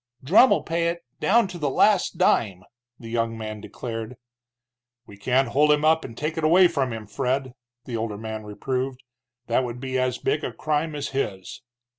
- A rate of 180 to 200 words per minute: Yes, average, 185 wpm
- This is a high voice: No, low, 130 Hz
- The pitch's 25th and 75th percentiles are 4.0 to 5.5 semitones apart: Yes, average, 5.0 semitones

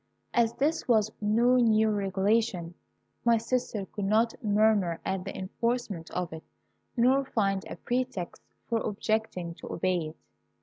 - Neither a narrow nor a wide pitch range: Yes, average, 3.5 semitones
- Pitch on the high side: Yes, high, 215 Hz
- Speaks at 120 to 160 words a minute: Yes, average, 140 wpm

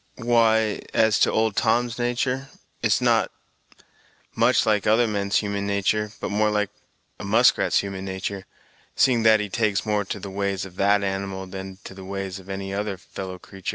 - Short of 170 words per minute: No, average, 190 wpm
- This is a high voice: No, low, 100 Hz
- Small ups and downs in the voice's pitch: Yes, narrow, 2.1 semitones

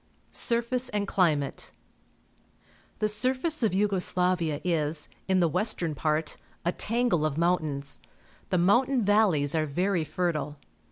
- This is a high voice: No, medium, 180 Hz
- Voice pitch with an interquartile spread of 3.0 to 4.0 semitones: No, wide, 5.4 semitones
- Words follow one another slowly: Yes, slow, 130 wpm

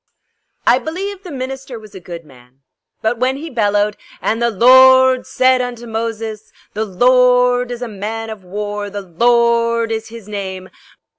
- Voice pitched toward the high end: Yes, high, 230 Hz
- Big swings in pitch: No, average, 3.4 semitones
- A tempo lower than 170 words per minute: Yes, average, 160 wpm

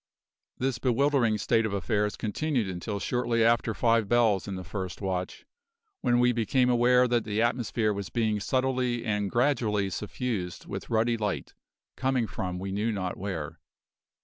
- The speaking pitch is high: No, low, 110 Hz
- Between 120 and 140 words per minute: No, average, 155 wpm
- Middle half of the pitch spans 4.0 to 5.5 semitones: No, average, 3.3 semitones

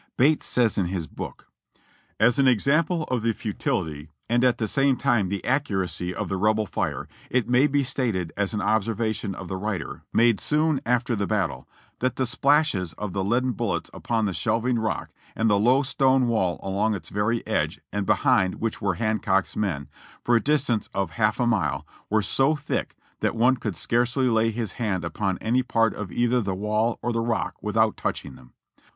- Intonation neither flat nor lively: Yes, average, 3.9 semitones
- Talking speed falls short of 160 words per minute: No, average, 200 wpm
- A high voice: No, low, 110 Hz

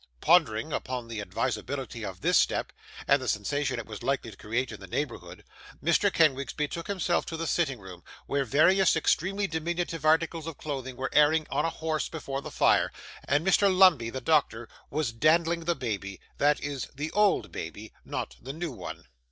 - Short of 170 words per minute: No, average, 185 wpm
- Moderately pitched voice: Yes, medium, 145 Hz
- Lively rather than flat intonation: Yes, wide, 5.7 semitones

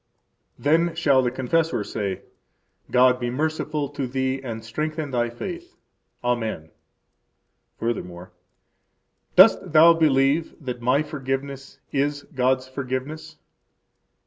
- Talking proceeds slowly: Yes, slow, 105 wpm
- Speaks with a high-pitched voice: No, low, 135 Hz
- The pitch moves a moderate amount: Yes, average, 3.8 semitones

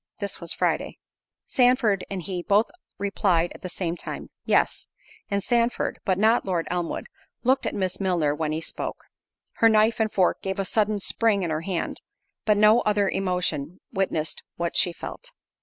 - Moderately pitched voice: No, high, 195 Hz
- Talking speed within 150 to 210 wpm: Yes, average, 175 wpm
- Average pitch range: Yes, average, 3.5 semitones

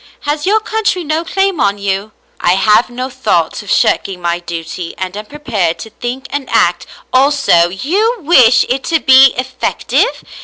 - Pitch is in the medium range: No, very high, 255 Hz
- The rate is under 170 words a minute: No, average, 185 wpm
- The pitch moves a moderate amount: No, wide, 7.3 semitones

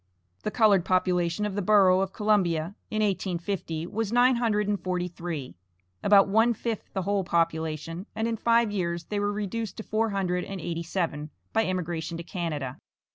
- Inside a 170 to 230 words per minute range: Yes, average, 180 wpm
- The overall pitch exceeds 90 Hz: Yes, high, 190 Hz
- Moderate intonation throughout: Yes, average, 3.6 semitones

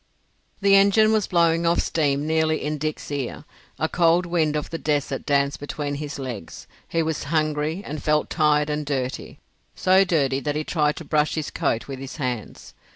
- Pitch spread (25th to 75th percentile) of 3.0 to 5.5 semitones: No, narrow, 2.5 semitones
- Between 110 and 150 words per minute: No, average, 180 wpm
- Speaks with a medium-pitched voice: Yes, medium, 150 Hz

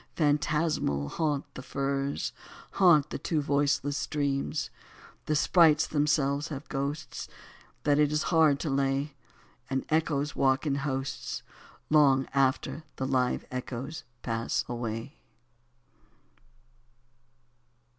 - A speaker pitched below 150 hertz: Yes, medium, 140 Hz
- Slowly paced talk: Yes, slow, 105 wpm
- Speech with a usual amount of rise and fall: No, narrow, 2.0 semitones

